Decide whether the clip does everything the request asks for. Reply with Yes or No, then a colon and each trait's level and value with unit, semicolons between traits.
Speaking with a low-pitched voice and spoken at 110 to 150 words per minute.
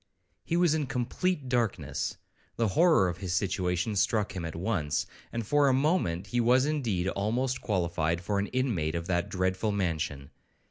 No: low, 100 Hz; average, 170 wpm